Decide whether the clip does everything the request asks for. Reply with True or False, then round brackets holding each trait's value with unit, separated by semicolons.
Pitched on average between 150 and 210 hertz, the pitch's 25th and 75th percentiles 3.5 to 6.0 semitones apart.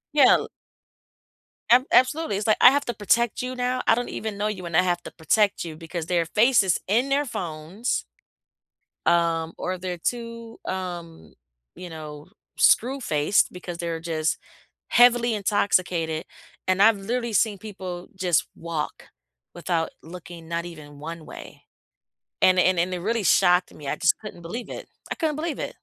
True (185 Hz; 5.5 semitones)